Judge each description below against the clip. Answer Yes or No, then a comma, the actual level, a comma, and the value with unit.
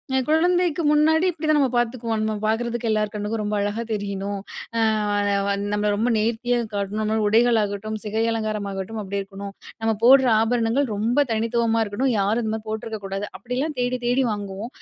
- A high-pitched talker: Yes, high, 225 Hz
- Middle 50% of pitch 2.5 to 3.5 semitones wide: Yes, average, 2.9 semitones